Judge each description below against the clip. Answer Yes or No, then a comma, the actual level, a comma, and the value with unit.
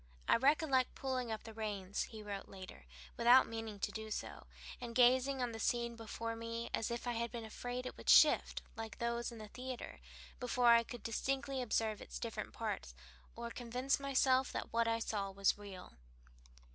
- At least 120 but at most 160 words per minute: No, average, 185 wpm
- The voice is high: Yes, high, 235 Hz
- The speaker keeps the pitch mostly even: Yes, narrow, 2.3 semitones